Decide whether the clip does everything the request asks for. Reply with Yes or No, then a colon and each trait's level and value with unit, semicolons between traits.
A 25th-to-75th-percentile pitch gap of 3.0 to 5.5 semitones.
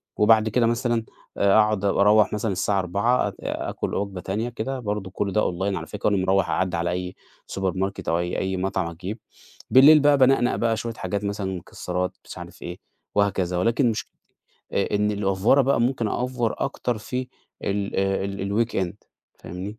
Yes: average, 3.3 semitones